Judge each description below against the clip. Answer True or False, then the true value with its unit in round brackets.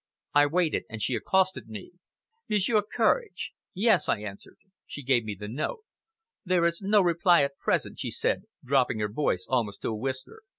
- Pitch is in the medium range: True (145 Hz)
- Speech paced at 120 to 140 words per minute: False (175 wpm)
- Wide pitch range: True (8.8 semitones)